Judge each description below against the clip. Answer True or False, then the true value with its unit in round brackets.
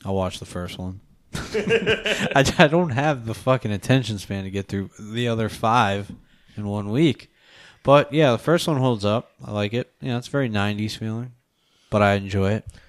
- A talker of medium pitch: False (115 Hz)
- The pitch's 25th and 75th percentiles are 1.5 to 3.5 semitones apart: False (4.8 semitones)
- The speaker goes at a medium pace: True (185 wpm)